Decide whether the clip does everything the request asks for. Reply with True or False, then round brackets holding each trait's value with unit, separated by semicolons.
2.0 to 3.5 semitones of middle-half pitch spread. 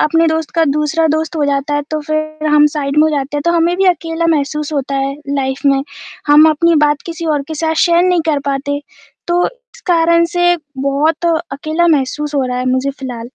True (2.8 semitones)